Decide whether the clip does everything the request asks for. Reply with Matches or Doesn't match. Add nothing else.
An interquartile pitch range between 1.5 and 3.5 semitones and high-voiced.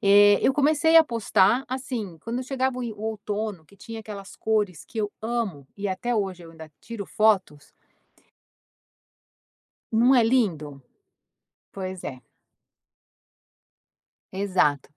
Doesn't match